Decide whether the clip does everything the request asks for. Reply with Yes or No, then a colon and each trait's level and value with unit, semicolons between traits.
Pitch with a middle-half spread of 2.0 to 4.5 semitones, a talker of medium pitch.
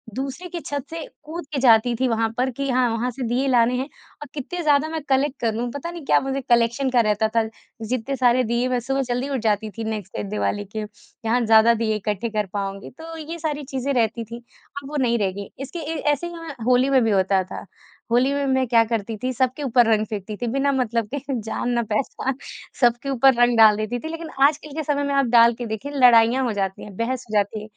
No: average, 3.6 semitones; high, 245 Hz